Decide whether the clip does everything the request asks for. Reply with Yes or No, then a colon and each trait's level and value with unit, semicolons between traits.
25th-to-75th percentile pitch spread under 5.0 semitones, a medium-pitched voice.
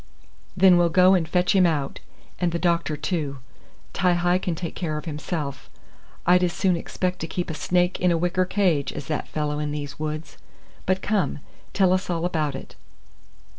Yes: average, 3.0 semitones; medium, 175 Hz